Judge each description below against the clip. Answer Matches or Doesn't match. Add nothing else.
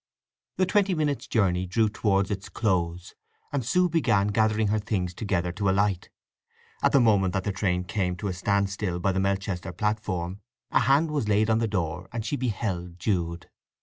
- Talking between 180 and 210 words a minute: Matches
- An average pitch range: Matches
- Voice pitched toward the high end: Doesn't match